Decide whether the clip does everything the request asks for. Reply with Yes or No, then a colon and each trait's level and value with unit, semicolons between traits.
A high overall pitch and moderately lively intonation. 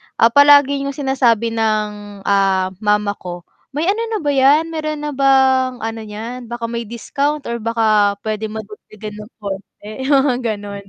Yes: high, 230 Hz; average, 4.6 semitones